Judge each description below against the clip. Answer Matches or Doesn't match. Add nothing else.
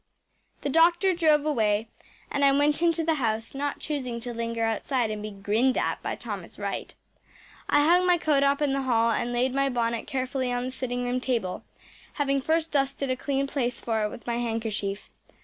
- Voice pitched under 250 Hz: Doesn't match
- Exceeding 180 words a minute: Matches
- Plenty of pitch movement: Doesn't match